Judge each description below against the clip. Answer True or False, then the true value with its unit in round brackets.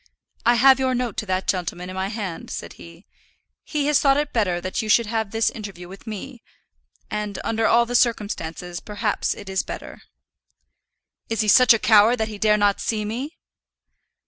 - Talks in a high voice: True (215 Hz)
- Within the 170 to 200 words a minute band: True (190 wpm)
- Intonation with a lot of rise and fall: False (3.5 semitones)